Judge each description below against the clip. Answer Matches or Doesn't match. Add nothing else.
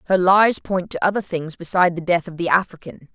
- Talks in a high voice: Doesn't match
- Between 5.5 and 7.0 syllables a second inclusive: Matches